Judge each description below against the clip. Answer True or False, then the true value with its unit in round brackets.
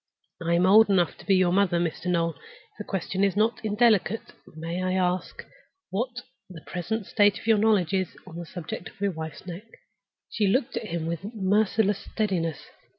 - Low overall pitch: False (190 Hz)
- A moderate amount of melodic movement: True (3.7 semitones)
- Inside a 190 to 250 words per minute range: True (195 wpm)